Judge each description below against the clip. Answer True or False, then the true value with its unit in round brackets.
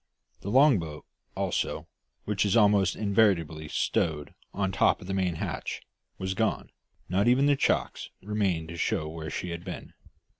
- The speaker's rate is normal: True (160 wpm)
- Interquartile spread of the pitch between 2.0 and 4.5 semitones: True (4.1 semitones)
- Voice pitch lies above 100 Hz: False (95 Hz)